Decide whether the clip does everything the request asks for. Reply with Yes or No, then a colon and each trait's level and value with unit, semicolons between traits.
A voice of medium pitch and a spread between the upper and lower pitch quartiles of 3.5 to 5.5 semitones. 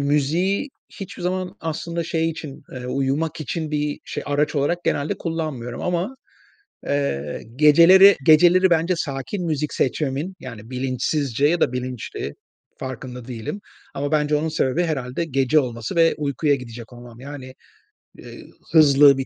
Yes: medium, 145 Hz; average, 4.0 semitones